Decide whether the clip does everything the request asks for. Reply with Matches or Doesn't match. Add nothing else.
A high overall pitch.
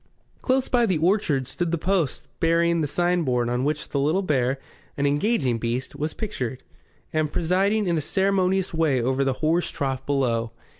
Doesn't match